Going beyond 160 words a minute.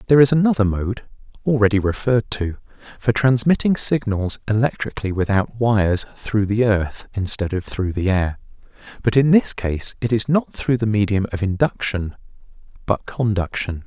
No: average, 150 wpm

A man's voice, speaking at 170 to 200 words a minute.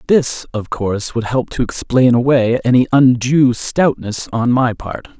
No: male; average, 160 wpm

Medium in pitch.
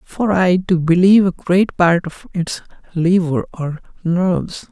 Yes: medium, 175 Hz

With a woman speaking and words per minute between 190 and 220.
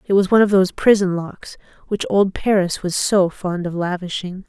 Yes: female; average, 200 wpm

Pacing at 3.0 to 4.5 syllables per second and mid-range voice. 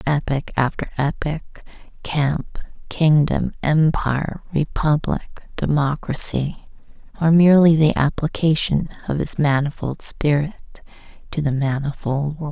Yes: 4.1 syllables/s; medium, 150 Hz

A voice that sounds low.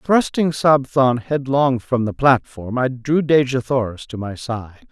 Yes: low, 130 Hz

